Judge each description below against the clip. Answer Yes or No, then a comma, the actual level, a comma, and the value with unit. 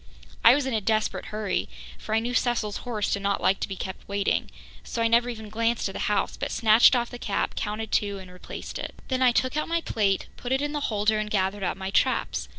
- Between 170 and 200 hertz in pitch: No, high, 215 Hz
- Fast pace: Yes, fast, 250 wpm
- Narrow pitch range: No, average, 3.1 semitones